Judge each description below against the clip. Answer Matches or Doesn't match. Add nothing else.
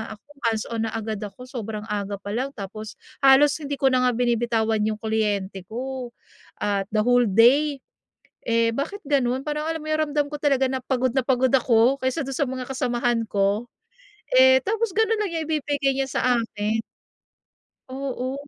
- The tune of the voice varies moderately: Matches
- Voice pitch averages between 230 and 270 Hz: Matches